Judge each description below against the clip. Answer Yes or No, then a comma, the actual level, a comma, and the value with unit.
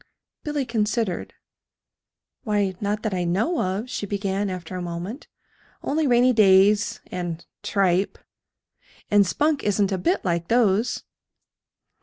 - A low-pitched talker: No, high, 205 Hz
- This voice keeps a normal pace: No, slow, 125 wpm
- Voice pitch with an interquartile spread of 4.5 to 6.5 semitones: No, average, 3.8 semitones